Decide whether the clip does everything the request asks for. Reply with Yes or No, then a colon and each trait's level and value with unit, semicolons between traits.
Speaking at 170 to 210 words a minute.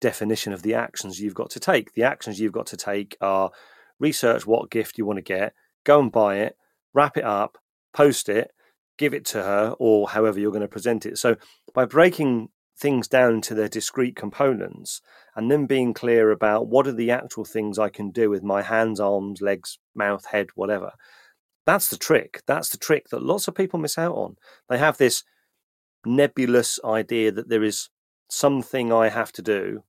Yes: average, 195 wpm